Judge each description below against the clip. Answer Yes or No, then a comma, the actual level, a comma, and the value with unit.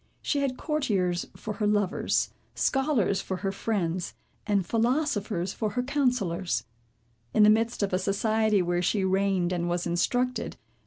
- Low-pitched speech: No, high, 205 Hz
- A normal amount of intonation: Yes, average, 4.4 semitones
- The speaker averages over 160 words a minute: No, average, 150 wpm